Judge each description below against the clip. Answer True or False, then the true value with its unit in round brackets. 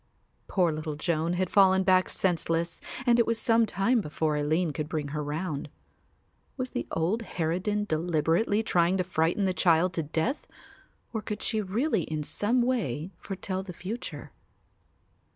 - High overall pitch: False (180 Hz)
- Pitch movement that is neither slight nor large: True (4.7 semitones)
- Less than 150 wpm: False (155 wpm)